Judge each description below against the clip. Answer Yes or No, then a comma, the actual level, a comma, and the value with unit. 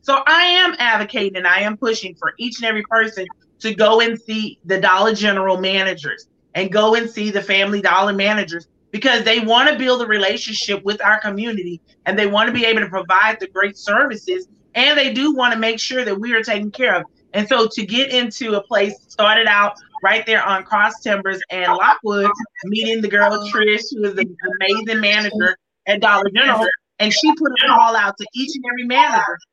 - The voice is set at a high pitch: Yes, high, 215 Hz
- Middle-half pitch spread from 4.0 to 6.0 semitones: No, average, 2.7 semitones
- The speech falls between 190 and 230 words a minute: Yes, fast, 205 wpm